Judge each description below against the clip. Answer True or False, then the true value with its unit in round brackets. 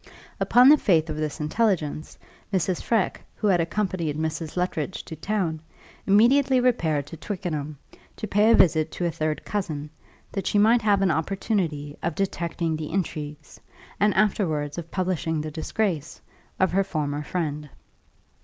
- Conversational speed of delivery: True (155 wpm)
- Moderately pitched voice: True (170 Hz)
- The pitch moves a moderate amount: True (4.6 semitones)